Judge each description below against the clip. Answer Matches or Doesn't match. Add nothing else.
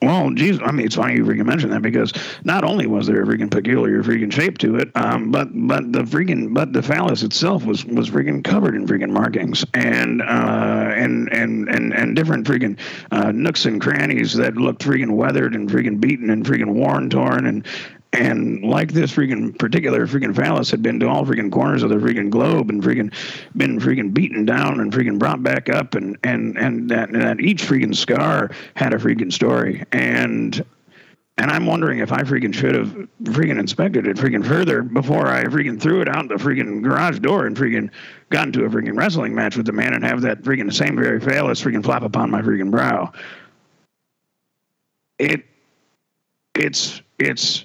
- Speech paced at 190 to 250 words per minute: Matches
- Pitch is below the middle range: Matches